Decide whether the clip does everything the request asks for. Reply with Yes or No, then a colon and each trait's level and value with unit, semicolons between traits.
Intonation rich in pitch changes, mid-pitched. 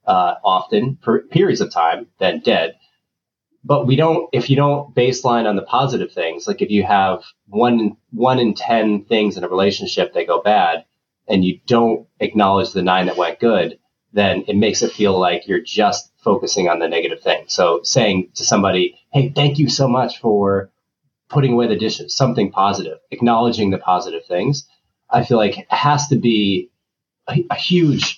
No: wide, 5.7 semitones; low, 115 Hz